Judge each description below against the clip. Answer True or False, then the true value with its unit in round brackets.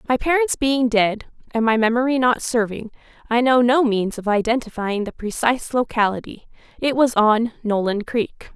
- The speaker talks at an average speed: True (160 wpm)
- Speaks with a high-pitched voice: True (235 Hz)